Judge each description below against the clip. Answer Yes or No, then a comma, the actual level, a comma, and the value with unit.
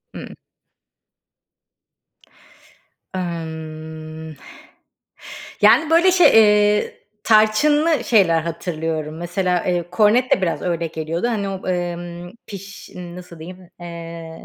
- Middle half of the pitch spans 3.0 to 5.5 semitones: Yes, average, 4.0 semitones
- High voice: No, medium, 175 Hz